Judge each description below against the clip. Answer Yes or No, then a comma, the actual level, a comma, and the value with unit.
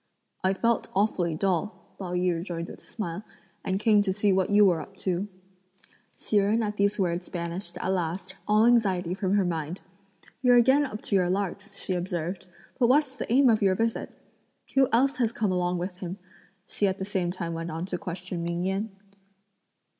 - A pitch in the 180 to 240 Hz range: Yes, high, 190 Hz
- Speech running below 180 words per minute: No, average, 195 wpm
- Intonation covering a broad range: No, average, 3.0 semitones